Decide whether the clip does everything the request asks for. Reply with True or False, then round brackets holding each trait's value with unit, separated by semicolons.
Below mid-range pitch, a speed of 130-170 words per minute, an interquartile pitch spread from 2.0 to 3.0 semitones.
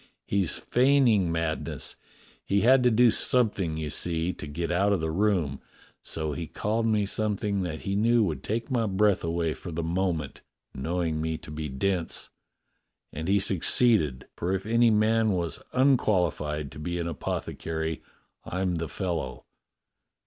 False (90 Hz; 160 wpm; 5.0 semitones)